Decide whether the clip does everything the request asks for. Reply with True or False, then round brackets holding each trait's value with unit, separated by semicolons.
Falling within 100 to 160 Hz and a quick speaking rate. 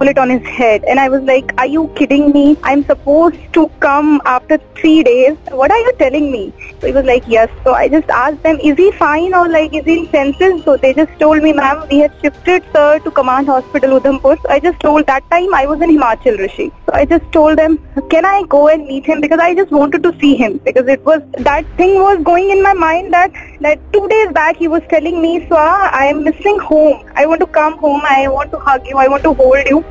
False (305 Hz; 250 wpm)